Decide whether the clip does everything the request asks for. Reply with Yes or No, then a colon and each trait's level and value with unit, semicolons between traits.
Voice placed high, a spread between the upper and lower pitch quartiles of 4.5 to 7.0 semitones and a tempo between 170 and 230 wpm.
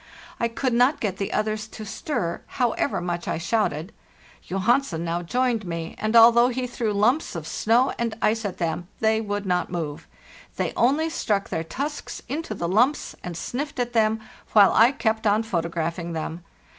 Yes: high, 215 Hz; wide, 5.5 semitones; average, 180 wpm